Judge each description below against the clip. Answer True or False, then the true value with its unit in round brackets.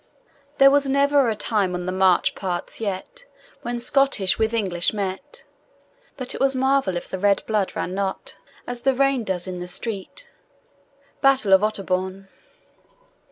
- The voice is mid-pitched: False (210 Hz)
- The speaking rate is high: False (160 wpm)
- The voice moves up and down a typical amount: False (6.0 semitones)